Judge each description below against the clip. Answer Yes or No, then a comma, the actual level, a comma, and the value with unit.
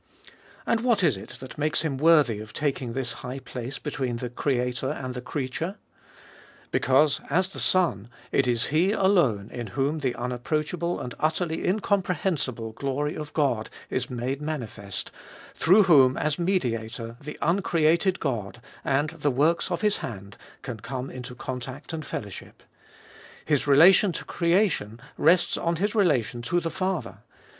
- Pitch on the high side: No, medium, 140 Hz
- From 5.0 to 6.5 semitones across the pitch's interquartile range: Yes, wide, 5.5 semitones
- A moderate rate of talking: Yes, average, 150 wpm